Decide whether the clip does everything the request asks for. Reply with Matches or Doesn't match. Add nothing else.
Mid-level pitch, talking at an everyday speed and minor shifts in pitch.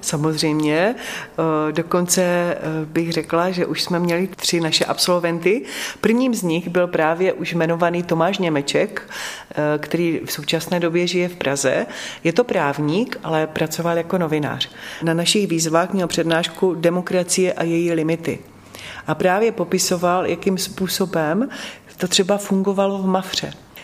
Matches